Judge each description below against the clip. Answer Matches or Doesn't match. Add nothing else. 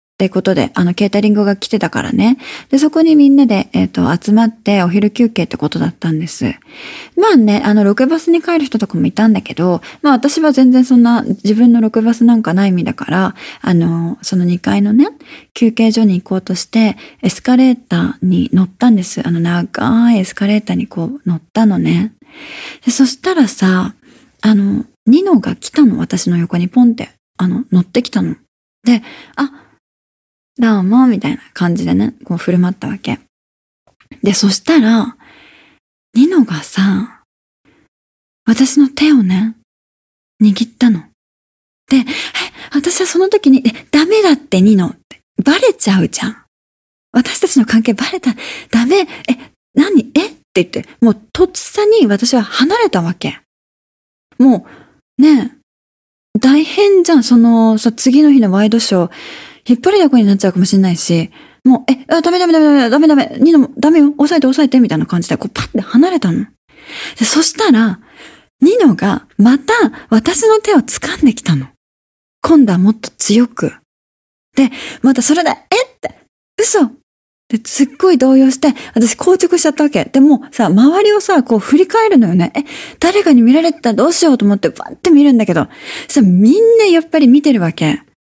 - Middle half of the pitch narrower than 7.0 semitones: Matches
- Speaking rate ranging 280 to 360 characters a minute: Matches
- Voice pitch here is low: Doesn't match